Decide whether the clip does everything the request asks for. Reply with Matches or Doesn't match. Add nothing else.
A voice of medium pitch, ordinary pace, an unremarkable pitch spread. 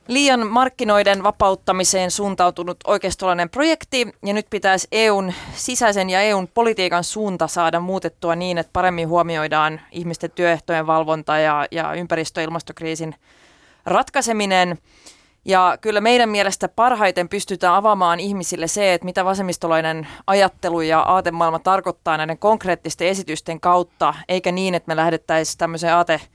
Matches